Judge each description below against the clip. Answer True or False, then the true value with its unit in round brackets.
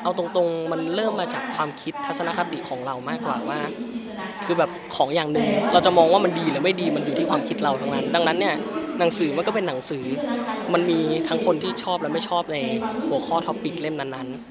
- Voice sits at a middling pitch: True (175 Hz)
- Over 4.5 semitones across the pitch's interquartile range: True (5.6 semitones)